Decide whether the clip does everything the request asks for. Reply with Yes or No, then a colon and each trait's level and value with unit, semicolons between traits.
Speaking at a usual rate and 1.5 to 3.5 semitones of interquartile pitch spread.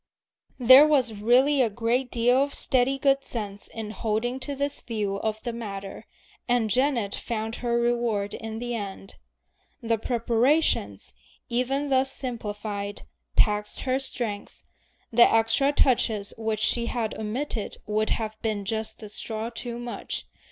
Yes: average, 145 wpm; average, 2.9 semitones